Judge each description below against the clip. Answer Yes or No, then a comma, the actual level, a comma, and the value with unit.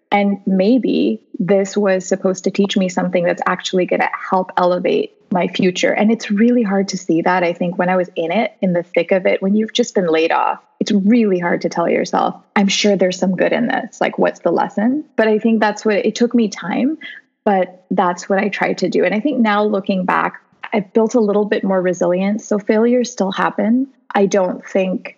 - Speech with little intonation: No, average, 3.4 semitones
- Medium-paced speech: No, fast, 225 wpm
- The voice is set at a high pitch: Yes, high, 200 Hz